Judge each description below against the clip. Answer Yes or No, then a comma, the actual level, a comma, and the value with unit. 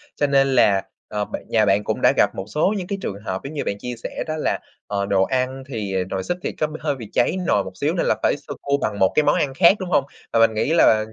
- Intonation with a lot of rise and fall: Yes, wide, 6.5 semitones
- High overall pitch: No, low, 120 Hz